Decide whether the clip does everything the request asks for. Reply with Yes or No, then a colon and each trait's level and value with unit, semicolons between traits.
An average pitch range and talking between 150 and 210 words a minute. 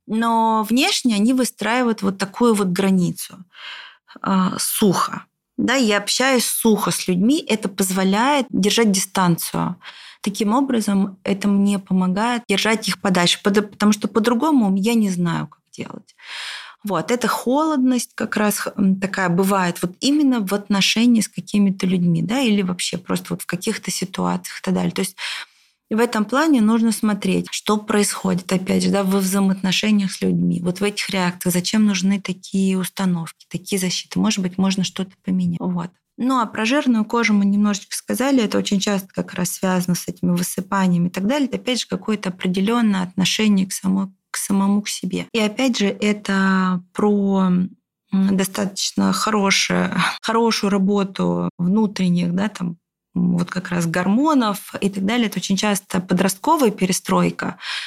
Yes: average, 3.0 semitones; average, 155 wpm